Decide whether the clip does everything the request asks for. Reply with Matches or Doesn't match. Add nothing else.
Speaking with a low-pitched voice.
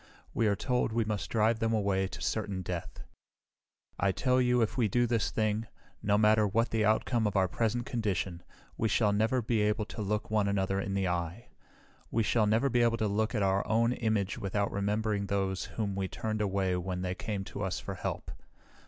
Matches